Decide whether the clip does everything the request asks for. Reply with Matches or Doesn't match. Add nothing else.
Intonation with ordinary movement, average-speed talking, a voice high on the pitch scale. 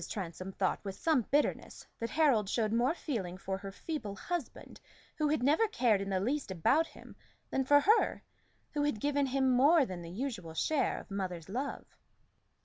Doesn't match